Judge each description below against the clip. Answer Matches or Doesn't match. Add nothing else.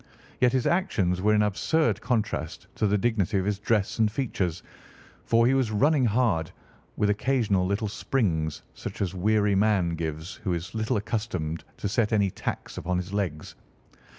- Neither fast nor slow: Matches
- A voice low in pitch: Matches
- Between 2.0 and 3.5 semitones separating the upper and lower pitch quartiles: Doesn't match